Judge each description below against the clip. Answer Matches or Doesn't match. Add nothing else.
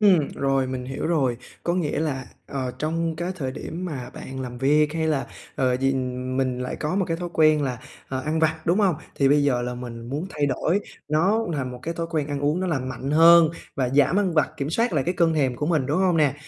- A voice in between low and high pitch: Matches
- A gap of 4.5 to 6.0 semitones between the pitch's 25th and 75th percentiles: Doesn't match